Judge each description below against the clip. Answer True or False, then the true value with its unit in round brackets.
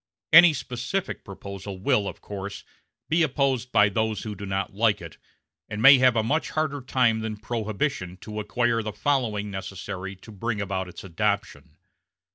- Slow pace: False (165 wpm)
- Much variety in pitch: False (4.2 semitones)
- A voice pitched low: True (110 Hz)